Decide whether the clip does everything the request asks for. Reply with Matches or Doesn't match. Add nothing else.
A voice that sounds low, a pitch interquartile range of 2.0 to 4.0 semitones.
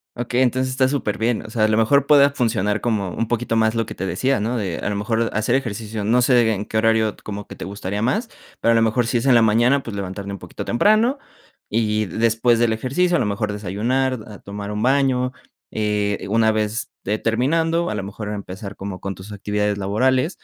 Matches